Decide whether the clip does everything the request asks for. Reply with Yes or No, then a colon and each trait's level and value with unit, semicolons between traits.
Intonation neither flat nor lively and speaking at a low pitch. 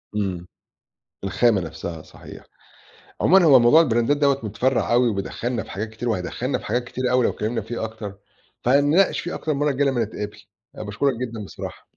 Yes: average, 4.2 semitones; low, 120 Hz